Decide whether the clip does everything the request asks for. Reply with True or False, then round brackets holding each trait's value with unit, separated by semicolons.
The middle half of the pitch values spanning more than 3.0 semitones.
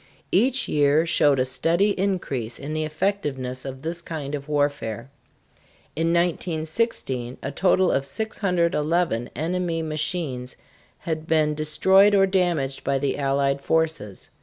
True (4.2 semitones)